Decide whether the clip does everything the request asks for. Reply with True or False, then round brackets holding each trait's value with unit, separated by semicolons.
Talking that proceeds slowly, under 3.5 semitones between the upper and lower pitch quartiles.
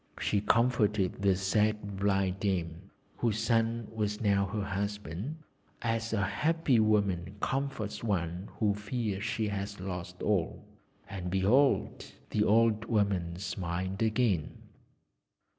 True (120 wpm; 2.6 semitones)